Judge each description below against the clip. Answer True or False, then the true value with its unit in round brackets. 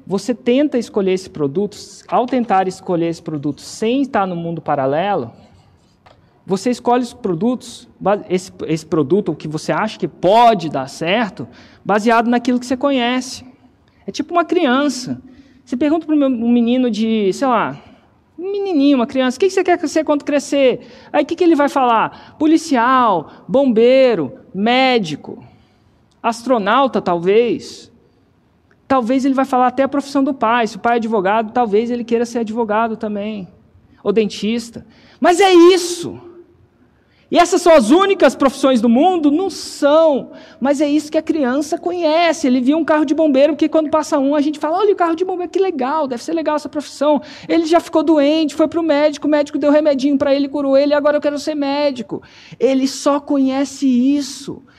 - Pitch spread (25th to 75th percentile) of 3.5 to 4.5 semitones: False (4.9 semitones)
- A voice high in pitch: True (270 Hz)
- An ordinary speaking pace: True (175 wpm)